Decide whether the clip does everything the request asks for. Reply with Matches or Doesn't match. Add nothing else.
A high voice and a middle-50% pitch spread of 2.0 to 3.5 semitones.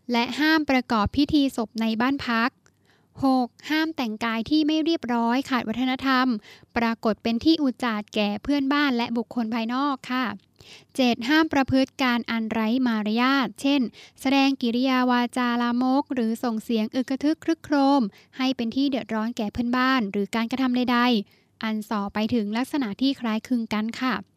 Matches